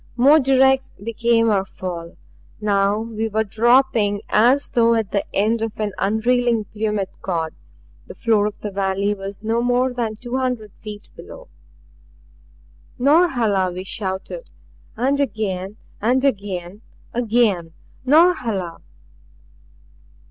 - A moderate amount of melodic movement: Yes, average, 3.6 semitones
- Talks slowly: Yes, slow, 120 wpm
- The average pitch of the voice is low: No, high, 220 Hz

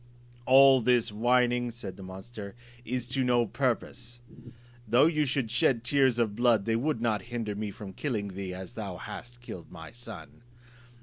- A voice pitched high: No, low, 120 Hz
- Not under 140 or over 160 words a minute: No, average, 170 wpm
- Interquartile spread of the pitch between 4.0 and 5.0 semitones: No, average, 3.2 semitones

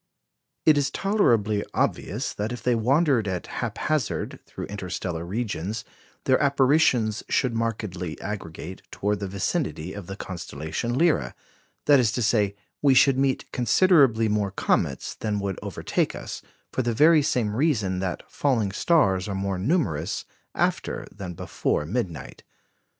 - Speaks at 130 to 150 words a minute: Yes, average, 140 wpm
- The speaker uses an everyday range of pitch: No, wide, 5.7 semitones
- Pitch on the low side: Yes, low, 110 Hz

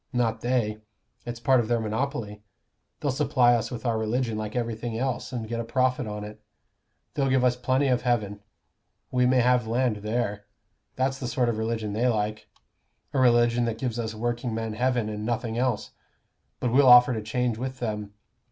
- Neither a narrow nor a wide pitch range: No, narrow, 2.3 semitones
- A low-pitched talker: Yes, low, 120 Hz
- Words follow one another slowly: No, average, 185 wpm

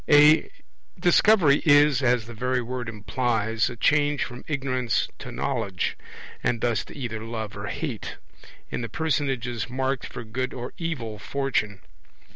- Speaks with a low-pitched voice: Yes, low, 125 Hz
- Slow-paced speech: No, average, 145 wpm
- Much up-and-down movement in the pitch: No, average, 3.6 semitones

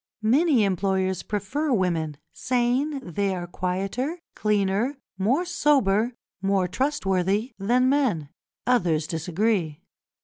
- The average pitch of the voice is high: Yes, high, 200 Hz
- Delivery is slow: Yes, slow, 100 wpm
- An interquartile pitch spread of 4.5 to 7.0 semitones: Yes, wide, 5.6 semitones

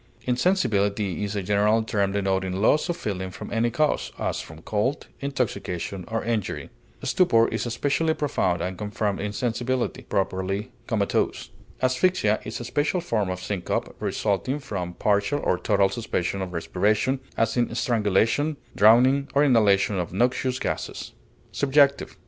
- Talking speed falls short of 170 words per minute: Yes, average, 140 wpm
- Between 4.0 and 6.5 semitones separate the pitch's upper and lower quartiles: Yes, average, 4.7 semitones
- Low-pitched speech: Yes, low, 110 Hz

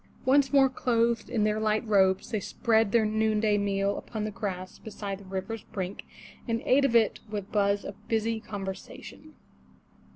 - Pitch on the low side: No, high, 215 Hz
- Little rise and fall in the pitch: Yes, narrow, 2.2 semitones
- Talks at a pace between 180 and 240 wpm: No, average, 165 wpm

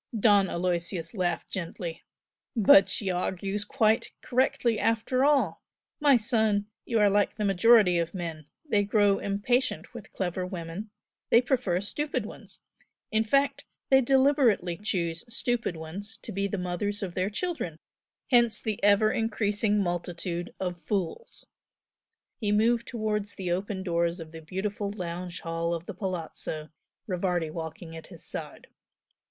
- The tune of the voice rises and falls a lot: No, average, 4.1 semitones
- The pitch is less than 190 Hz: No, high, 200 Hz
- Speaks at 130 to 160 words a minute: Yes, average, 145 wpm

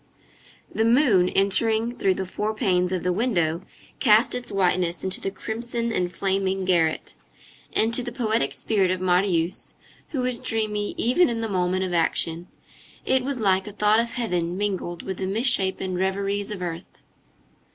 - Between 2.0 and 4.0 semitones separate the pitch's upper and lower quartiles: Yes, average, 3.7 semitones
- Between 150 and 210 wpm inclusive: Yes, average, 165 wpm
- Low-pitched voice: No, high, 195 Hz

